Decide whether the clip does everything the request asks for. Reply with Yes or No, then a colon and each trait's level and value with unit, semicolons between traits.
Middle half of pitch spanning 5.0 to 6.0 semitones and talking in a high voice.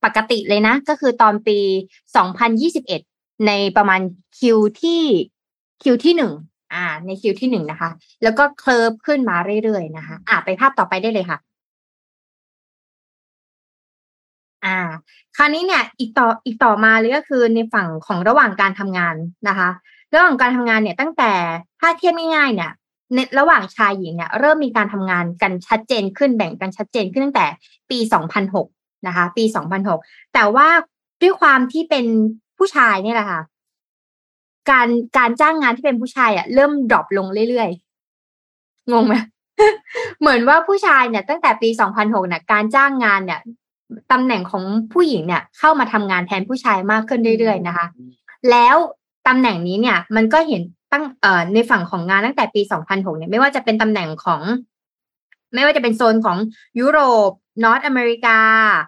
Yes: wide, 5.4 semitones; high, 225 Hz